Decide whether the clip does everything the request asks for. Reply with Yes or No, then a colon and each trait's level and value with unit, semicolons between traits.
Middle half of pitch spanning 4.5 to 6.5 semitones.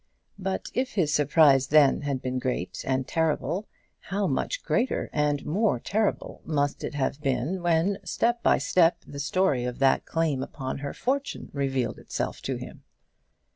Yes: wide, 5.6 semitones